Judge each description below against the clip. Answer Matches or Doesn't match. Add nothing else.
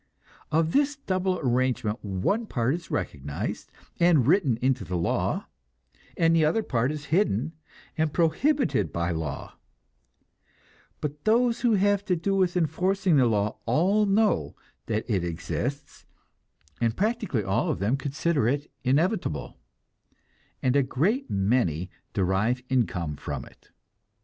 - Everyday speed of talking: Doesn't match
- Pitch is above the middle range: Doesn't match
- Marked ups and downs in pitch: Matches